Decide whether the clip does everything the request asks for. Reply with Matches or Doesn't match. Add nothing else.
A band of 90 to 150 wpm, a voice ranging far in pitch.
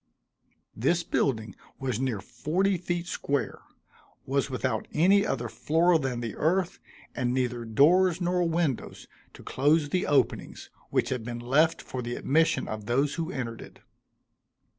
Matches